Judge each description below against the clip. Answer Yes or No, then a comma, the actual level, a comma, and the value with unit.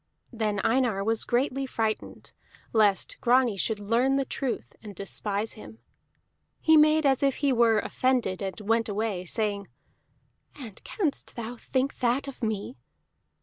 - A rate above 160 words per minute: No, average, 145 wpm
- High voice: Yes, high, 230 Hz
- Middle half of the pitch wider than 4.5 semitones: No, average, 3.9 semitones